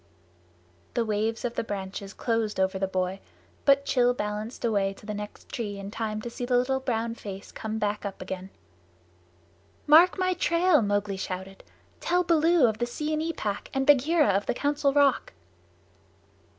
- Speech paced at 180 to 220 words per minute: No, average, 165 wpm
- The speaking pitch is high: Yes, high, 225 Hz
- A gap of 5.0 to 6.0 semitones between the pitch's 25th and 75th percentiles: Yes, wide, 5.5 semitones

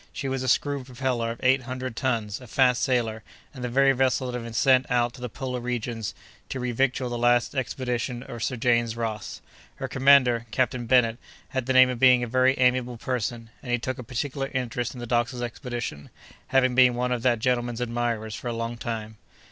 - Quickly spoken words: Yes, fast, 210 wpm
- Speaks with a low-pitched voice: Yes, low, 125 Hz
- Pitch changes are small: Yes, narrow, 1.5 semitones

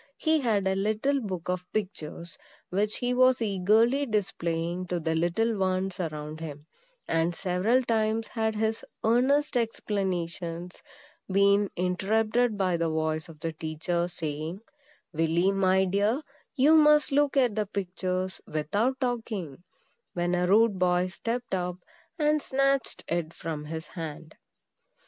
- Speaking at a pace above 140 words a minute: No, slow, 135 wpm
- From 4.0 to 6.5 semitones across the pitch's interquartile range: Yes, average, 4.8 semitones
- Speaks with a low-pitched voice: No, high, 190 Hz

